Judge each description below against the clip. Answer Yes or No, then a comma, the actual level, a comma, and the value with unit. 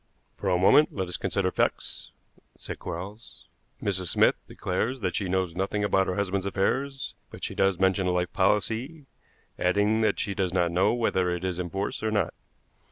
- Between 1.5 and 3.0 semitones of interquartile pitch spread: Yes, narrow, 2.4 semitones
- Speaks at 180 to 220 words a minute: Yes, average, 185 wpm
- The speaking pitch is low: Yes, very low, 95 Hz